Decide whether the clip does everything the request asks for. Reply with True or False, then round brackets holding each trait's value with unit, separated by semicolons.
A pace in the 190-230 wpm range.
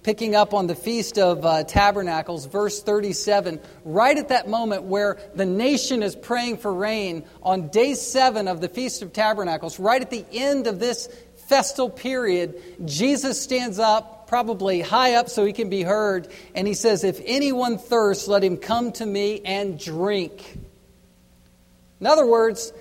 False (170 wpm)